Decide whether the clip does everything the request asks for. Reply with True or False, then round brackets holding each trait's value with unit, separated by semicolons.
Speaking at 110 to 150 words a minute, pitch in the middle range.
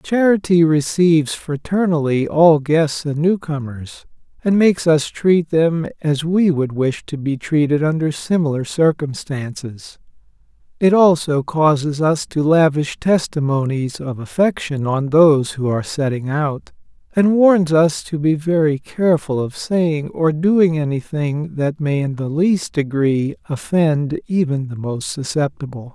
True (140 wpm; 155 Hz)